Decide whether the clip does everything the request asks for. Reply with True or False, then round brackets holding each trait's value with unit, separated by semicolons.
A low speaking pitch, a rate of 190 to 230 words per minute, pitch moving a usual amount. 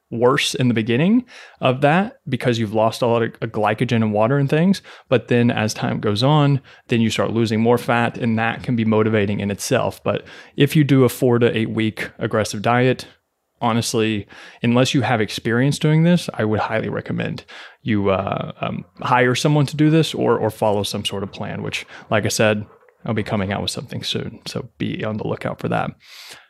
True (120 Hz; 205 wpm; 3.7 semitones)